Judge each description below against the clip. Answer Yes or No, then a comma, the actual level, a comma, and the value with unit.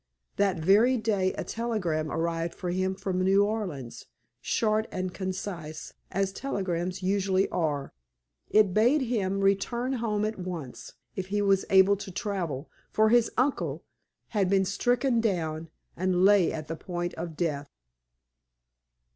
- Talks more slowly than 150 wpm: Yes, average, 140 wpm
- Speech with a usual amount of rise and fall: Yes, average, 3.4 semitones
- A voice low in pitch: No, high, 190 Hz